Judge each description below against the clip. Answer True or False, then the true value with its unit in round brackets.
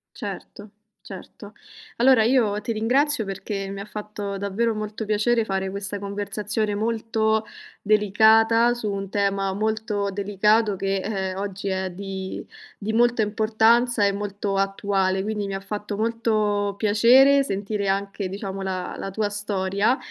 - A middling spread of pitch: False (1.9 semitones)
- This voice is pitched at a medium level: False (205 Hz)